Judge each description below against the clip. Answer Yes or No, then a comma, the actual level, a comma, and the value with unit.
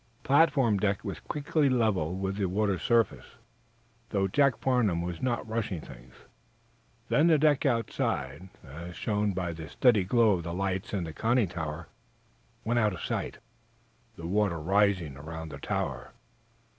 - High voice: No, low, 100 Hz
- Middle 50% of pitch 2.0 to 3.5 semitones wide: No, wide, 5.6 semitones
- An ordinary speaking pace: Yes, average, 155 wpm